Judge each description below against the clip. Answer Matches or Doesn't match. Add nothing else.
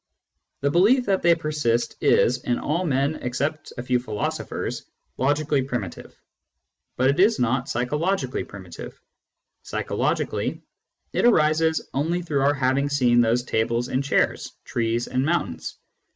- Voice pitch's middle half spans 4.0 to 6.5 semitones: Matches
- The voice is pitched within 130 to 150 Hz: Matches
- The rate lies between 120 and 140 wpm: Matches